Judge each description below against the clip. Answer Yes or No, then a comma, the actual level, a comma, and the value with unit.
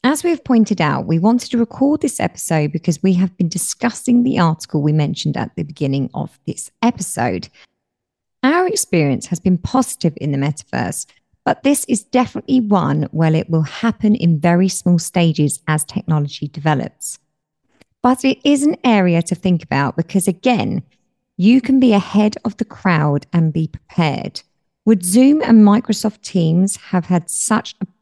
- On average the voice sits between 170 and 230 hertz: Yes, medium, 185 Hz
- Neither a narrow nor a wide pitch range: No, wide, 6.5 semitones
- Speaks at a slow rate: No, average, 170 wpm